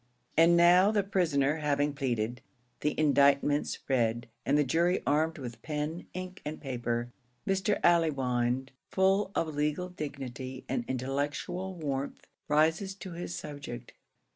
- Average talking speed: No, slow, 130 wpm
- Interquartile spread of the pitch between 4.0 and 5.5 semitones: Yes, average, 4.5 semitones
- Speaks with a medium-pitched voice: Yes, medium, 150 Hz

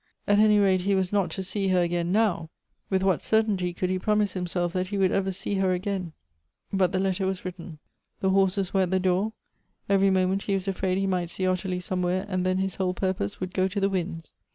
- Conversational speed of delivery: No, fast, 245 wpm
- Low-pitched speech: No, medium, 185 Hz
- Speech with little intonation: Yes, narrow, 1.2 semitones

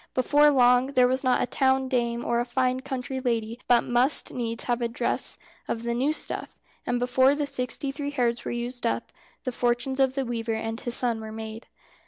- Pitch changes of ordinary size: No, narrow, 1.9 semitones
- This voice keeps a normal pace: No, fast, 210 wpm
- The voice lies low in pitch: No, high, 245 Hz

